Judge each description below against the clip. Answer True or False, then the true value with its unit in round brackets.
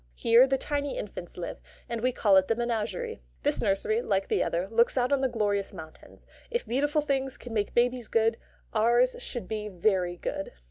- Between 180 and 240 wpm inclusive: True (190 wpm)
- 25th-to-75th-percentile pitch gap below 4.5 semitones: True (4.0 semitones)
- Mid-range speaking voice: False (230 Hz)